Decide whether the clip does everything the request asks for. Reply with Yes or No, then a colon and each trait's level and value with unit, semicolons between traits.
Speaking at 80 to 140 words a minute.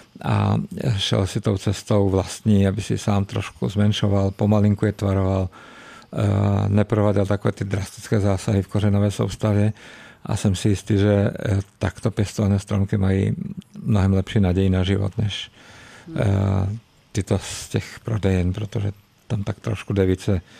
Yes: average, 135 wpm